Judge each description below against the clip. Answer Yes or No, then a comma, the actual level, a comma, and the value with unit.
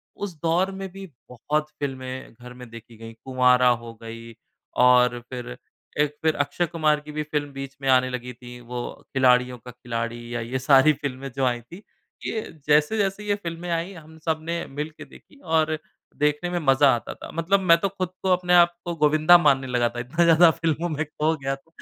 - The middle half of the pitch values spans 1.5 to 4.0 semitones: No, average, 5.0 semitones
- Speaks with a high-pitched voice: No, medium, 150 Hz